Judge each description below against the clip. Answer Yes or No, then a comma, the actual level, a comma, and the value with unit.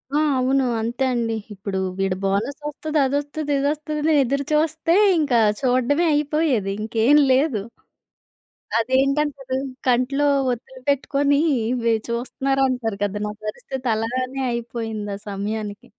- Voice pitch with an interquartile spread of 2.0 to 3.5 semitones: No, average, 4.1 semitones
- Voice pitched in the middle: No, very high, 255 Hz